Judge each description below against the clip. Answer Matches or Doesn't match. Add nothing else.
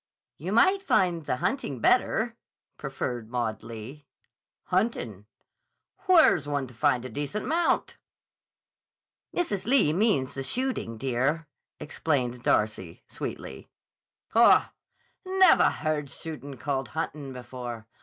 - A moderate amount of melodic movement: Doesn't match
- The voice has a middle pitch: Matches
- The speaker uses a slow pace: Matches